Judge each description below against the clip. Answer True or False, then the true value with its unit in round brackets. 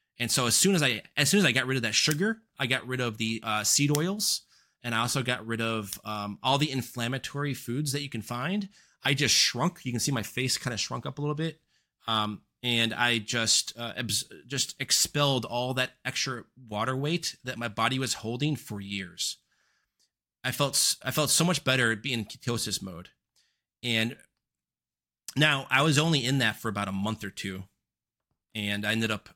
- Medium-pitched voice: False (125 Hz)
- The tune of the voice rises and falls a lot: False (4.1 semitones)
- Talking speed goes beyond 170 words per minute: True (205 wpm)